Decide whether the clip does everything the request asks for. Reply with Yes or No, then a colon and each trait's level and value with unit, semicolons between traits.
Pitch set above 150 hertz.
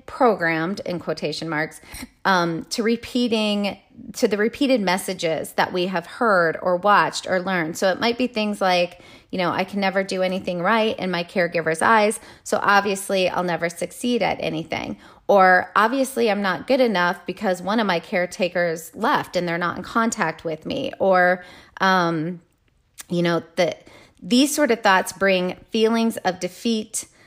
Yes: medium, 185 Hz